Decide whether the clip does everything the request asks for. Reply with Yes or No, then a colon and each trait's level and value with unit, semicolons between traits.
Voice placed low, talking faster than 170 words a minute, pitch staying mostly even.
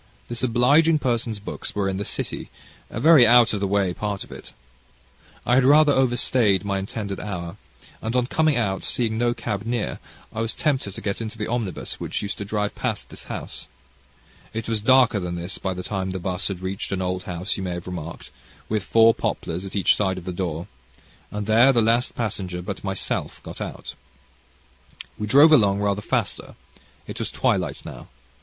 No: low, 105 Hz; average, 200 wpm; average, 3.9 semitones